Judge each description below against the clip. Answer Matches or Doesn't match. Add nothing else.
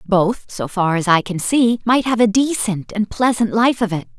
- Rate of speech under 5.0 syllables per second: Matches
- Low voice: Doesn't match